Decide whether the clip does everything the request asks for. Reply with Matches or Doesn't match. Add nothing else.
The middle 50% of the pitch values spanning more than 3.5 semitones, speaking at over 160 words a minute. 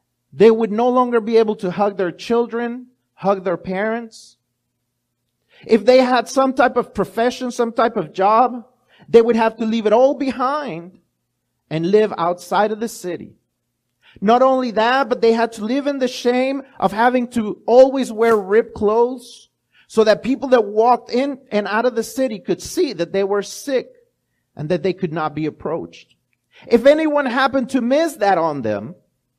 Matches